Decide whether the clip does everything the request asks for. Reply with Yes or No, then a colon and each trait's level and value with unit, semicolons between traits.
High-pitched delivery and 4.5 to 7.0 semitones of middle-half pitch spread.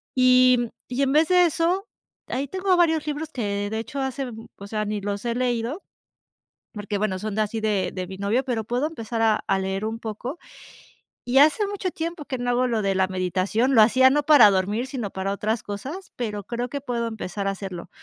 Yes: high, 235 Hz; average, 5.1 semitones